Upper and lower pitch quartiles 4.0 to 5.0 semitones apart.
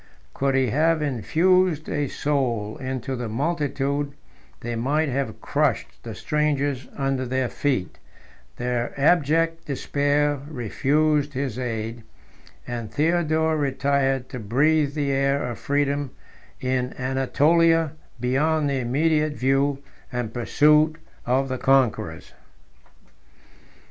No: average, 2.9 semitones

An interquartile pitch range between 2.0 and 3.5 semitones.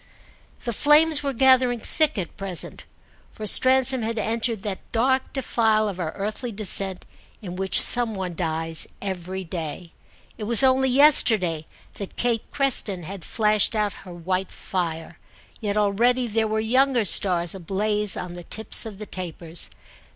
No: average, 4.7 semitones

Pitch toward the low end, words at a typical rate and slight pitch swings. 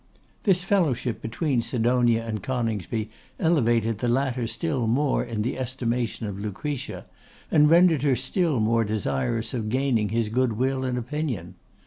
No: low, 120 Hz; average, 145 wpm; average, 3.3 semitones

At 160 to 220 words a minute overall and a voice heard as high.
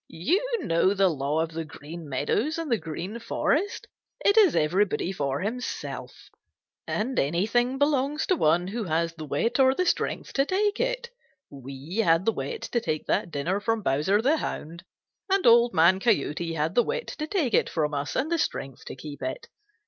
Yes: average, 185 wpm; high, 200 Hz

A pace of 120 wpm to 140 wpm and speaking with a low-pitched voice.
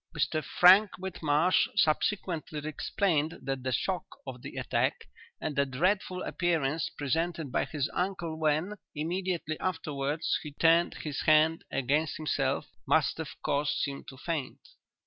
No: slow, 135 wpm; medium, 155 Hz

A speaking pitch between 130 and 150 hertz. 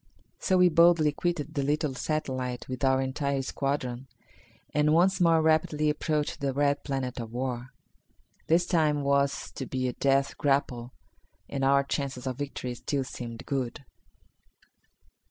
Yes: medium, 140 Hz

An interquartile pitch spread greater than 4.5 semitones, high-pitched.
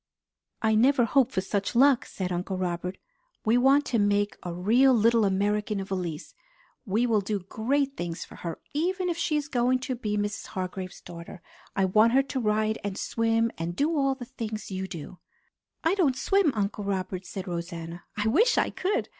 Yes: wide, 5.5 semitones; high, 215 Hz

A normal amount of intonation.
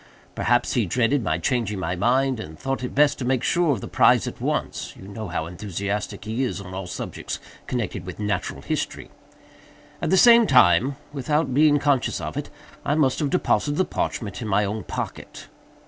No: wide, 6.1 semitones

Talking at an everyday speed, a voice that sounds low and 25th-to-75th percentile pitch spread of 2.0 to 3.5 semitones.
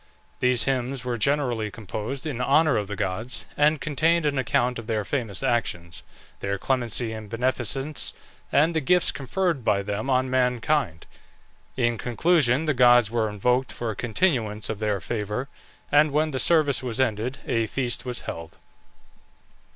No: average, 160 wpm; low, 125 Hz; average, 4.0 semitones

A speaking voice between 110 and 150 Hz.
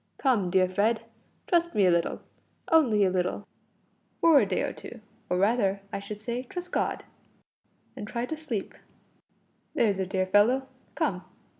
No: high, 210 Hz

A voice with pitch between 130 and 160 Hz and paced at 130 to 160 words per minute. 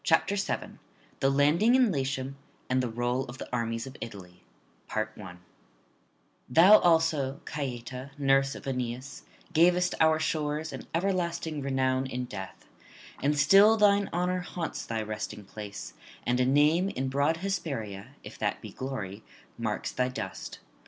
Yes: low, 135 Hz; average, 140 wpm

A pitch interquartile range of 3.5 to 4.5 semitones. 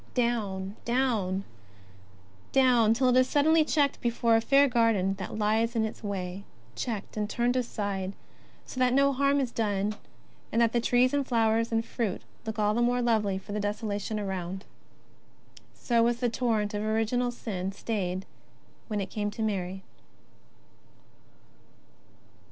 No: average, 3.1 semitones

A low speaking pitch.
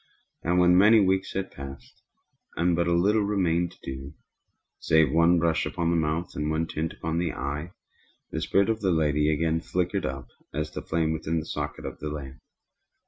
Yes: very low, 80 Hz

